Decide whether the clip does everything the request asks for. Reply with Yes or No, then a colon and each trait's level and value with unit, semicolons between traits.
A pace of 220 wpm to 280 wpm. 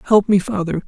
No: fast, 205 wpm